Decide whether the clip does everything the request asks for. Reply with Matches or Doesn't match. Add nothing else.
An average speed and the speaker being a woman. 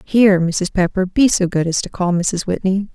Doesn't match